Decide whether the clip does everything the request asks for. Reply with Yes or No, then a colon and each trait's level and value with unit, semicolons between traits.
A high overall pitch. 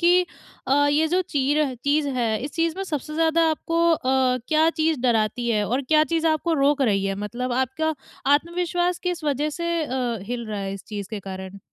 Yes: very high, 285 Hz